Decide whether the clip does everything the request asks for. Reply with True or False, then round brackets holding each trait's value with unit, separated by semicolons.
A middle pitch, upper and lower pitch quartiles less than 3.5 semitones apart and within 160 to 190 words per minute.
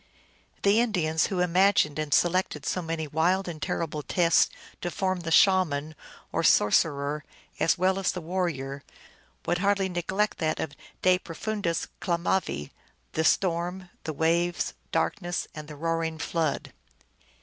False (170 Hz; 2.8 semitones; 140 wpm)